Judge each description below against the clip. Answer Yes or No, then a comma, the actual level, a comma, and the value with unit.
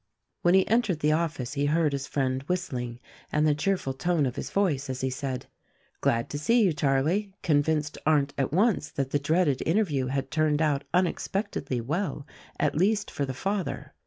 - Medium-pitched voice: Yes, medium, 150 Hz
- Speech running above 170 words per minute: Yes, average, 185 wpm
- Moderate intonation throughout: Yes, average, 4.7 semitones